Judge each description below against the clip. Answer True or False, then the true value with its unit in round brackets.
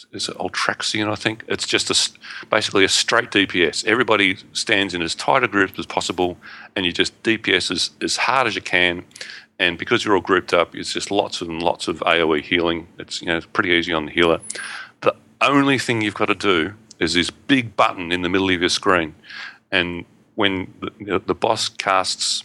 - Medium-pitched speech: False (95 Hz)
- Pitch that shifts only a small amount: False (3.6 semitones)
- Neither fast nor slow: False (210 wpm)